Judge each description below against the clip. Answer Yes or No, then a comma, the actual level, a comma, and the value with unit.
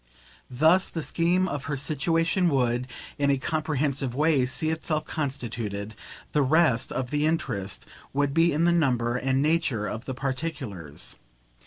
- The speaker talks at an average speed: Yes, average, 150 wpm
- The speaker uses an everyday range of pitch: Yes, average, 4.2 semitones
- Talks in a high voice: No, medium, 140 Hz